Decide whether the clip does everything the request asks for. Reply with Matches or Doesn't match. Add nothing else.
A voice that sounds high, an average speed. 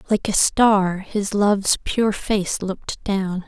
Matches